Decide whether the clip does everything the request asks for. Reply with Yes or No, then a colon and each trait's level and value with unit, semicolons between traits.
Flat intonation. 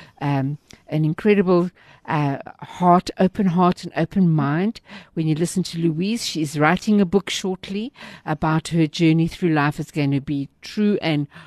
No: average, 3.3 semitones